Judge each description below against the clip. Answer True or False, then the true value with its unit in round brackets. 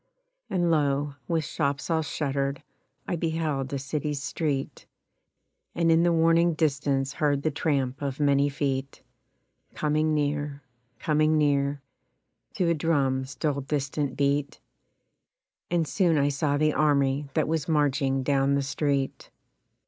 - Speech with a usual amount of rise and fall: False (2.0 semitones)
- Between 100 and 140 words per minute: True (135 wpm)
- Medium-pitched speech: True (145 Hz)